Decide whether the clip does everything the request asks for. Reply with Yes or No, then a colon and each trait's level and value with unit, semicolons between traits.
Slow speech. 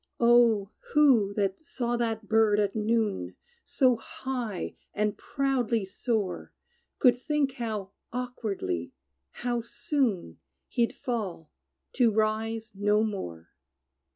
Yes: slow, 105 wpm